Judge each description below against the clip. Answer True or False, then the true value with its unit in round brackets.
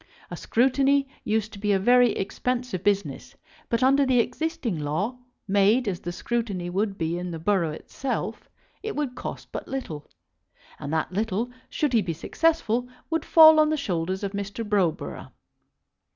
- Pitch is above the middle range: True (215 Hz)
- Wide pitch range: True (5.7 semitones)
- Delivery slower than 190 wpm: True (165 wpm)